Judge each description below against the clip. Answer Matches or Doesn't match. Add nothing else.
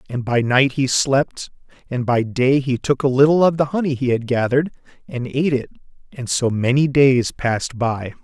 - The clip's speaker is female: Doesn't match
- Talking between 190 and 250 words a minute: Matches